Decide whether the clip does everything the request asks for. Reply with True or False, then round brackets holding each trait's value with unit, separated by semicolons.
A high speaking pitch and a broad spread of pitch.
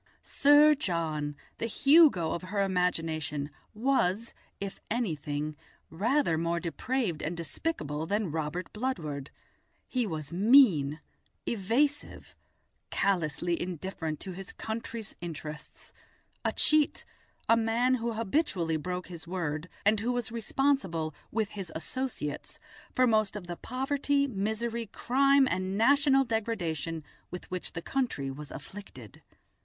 True (195 Hz; 6.7 semitones)